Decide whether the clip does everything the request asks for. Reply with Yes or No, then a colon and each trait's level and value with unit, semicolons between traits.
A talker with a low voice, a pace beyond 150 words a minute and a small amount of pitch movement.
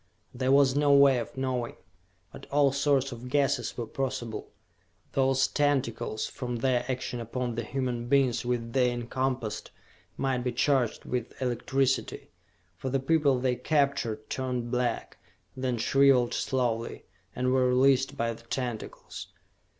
No: low, 130 Hz; average, 140 wpm; narrow, 2.0 semitones